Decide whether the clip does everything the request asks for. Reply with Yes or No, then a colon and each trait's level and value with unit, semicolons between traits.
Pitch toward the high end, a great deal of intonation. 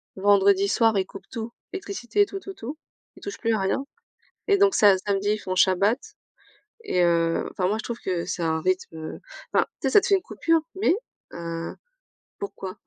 Yes: high, 200 Hz; wide, 6.3 semitones